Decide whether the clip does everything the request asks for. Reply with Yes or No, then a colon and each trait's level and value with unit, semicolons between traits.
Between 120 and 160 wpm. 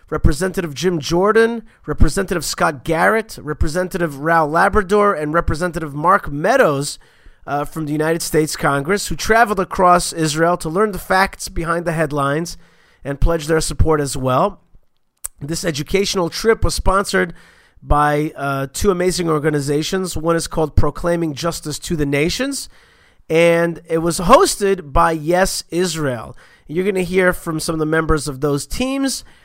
Yes: average, 150 wpm